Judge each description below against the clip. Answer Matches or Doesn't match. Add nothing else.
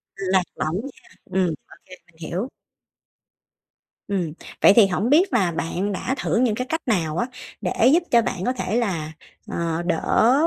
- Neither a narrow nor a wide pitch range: Doesn't match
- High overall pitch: Matches